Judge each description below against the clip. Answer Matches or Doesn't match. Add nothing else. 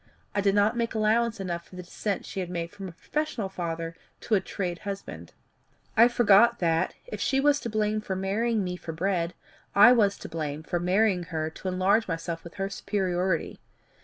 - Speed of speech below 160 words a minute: Doesn't match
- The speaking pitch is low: Doesn't match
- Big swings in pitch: Doesn't match